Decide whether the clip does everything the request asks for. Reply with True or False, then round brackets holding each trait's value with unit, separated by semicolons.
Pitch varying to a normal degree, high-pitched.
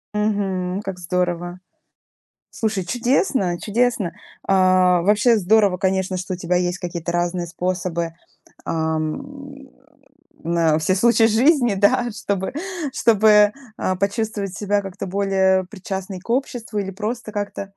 True (3.1 semitones; 195 Hz)